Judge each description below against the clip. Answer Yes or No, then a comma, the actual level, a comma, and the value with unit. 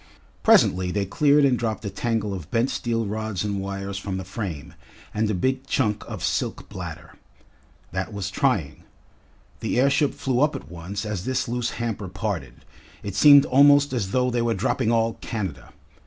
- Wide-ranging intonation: No, average, 4.3 semitones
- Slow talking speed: No, average, 175 wpm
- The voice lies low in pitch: Yes, low, 110 Hz